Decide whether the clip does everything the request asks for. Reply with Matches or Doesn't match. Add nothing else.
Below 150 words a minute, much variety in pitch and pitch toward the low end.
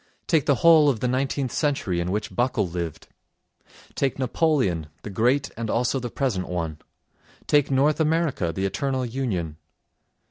Matches